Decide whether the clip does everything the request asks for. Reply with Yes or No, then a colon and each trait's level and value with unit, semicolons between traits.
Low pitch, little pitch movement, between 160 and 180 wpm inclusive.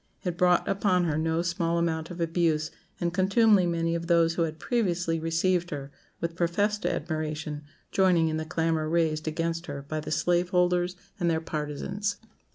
No: medium, 170 Hz; narrow, 1.9 semitones; average, 170 wpm